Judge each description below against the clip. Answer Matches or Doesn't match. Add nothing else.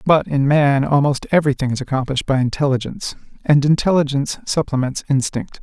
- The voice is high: Doesn't match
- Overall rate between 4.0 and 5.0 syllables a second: Doesn't match